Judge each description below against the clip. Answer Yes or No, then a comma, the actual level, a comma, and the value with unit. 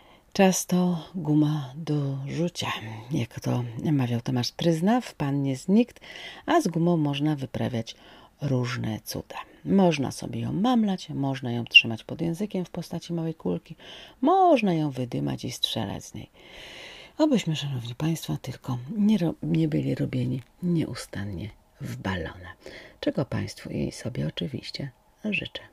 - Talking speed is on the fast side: No, average, 135 wpm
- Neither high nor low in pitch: Yes, medium, 150 Hz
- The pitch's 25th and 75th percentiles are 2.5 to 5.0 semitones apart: No, wide, 5.6 semitones